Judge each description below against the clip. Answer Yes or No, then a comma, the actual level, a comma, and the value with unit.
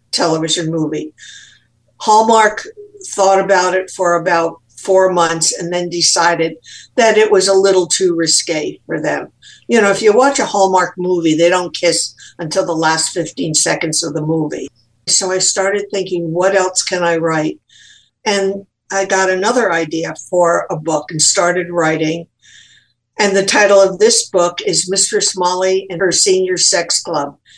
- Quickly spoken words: No, average, 165 wpm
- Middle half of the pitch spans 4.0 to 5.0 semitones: No, average, 2.8 semitones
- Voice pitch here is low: No, medium, 180 Hz